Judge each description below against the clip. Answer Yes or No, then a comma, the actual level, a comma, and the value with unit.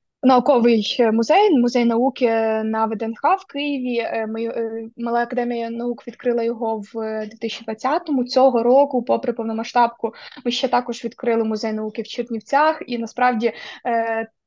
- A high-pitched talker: Yes, high, 235 Hz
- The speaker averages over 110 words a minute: Yes, average, 120 wpm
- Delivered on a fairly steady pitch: Yes, narrow, 1.8 semitones